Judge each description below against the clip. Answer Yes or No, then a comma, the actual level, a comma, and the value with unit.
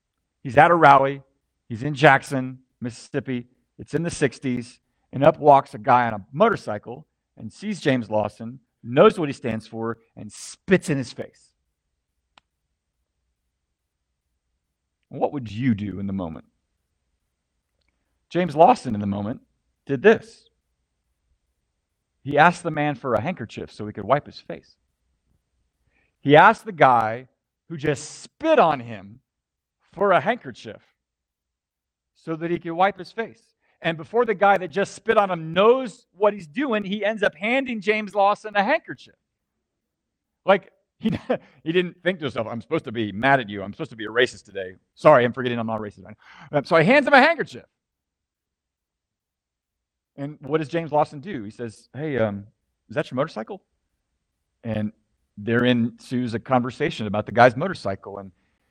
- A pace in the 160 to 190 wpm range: Yes, average, 165 wpm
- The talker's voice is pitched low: Yes, low, 120 Hz